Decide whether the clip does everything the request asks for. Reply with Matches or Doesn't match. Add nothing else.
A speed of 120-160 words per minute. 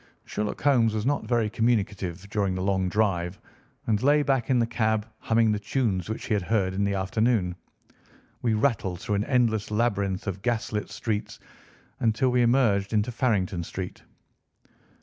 Doesn't match